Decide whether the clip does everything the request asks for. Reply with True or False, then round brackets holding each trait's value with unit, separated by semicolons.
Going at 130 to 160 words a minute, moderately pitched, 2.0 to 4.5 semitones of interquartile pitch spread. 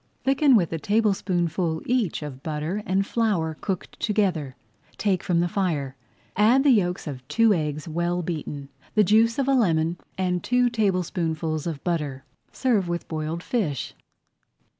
False (150 wpm; 175 Hz; 5.0 semitones)